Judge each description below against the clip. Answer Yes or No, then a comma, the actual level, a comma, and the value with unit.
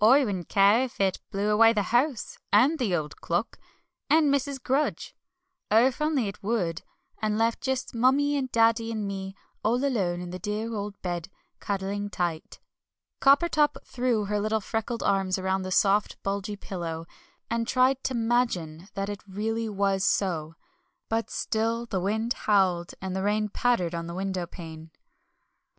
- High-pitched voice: Yes, high, 210 Hz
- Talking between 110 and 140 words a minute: No, average, 165 wpm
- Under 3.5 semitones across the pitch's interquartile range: No, average, 3.8 semitones